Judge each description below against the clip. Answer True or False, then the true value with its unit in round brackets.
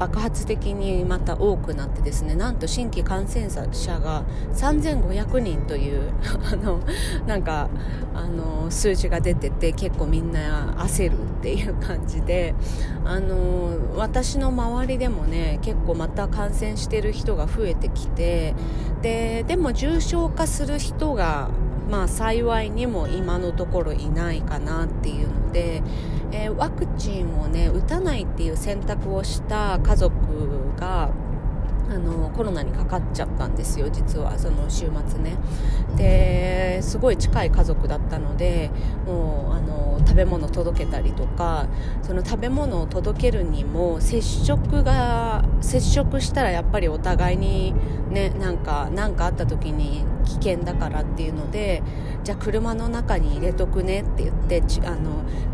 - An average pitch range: True (4.3 semitones)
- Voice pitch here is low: True (105 Hz)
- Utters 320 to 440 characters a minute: False (270 characters per minute)